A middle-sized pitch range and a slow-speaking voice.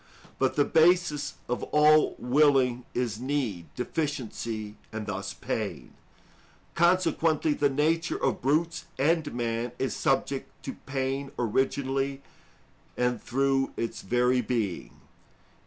Yes: average, 4.0 semitones; slow, 110 wpm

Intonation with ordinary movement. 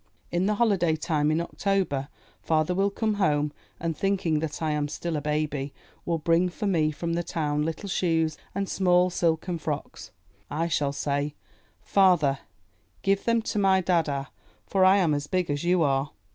Yes: average, 3.9 semitones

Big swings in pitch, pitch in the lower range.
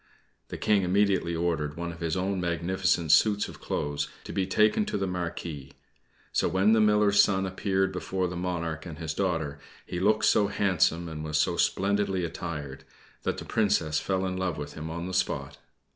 No: average, 3.2 semitones; very low, 90 Hz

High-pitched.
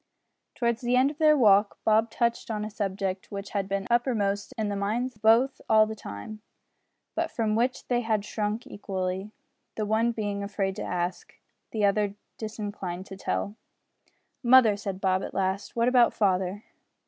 Yes: high, 210 Hz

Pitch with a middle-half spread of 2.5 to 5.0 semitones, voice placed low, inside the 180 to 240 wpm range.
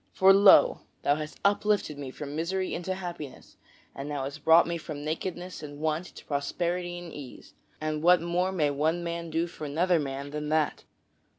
No: average, 3.0 semitones; medium, 160 Hz; average, 185 wpm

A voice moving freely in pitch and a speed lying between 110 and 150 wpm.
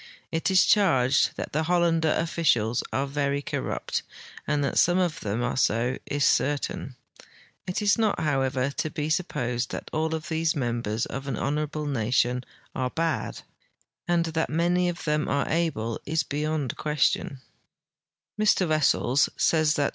No: average, 3.9 semitones; average, 145 wpm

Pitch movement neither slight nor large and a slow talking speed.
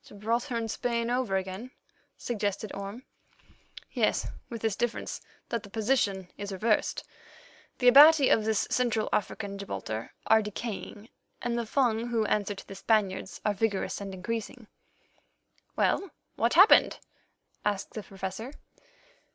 Yes: average, 3.1 semitones; slow, 130 wpm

